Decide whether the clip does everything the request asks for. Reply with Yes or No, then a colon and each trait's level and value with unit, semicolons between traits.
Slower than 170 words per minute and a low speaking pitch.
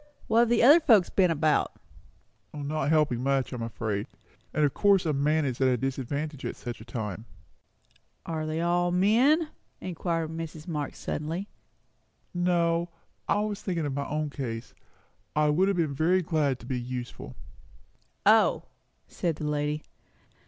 No: average, 160 wpm; medium, 155 Hz